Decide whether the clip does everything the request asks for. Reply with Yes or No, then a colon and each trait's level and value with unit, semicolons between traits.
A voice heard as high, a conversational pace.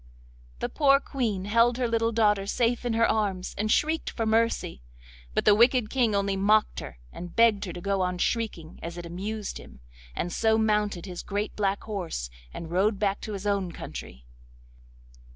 Yes: high, 210 Hz; average, 185 wpm